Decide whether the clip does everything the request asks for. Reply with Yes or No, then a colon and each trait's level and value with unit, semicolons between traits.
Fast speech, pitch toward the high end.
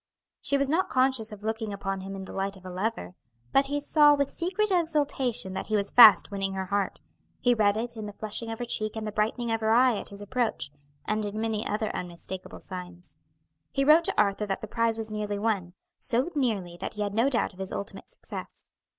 Yes: fast, 230 wpm; high, 215 Hz